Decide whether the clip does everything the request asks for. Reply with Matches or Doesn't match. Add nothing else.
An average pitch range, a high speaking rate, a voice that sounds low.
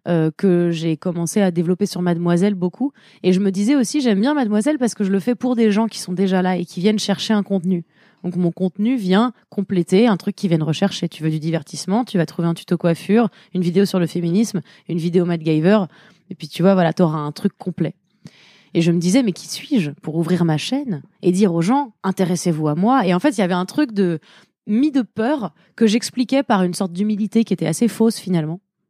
Doesn't match